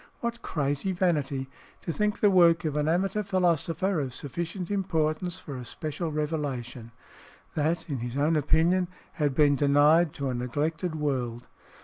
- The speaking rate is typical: Yes, average, 150 wpm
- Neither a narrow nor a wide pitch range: Yes, average, 3.7 semitones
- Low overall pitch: No, medium, 155 Hz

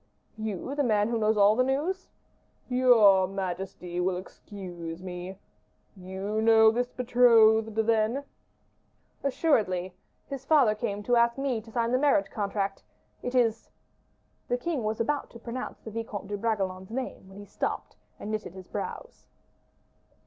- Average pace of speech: Yes, average, 150 wpm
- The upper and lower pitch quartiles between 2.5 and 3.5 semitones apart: No, average, 4.0 semitones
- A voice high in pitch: Yes, high, 220 Hz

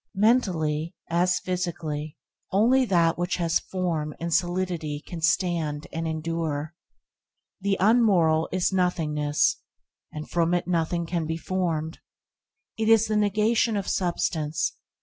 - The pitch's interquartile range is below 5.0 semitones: Yes, average, 2.9 semitones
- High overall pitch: No, medium, 175 Hz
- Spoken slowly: Yes, slow, 125 wpm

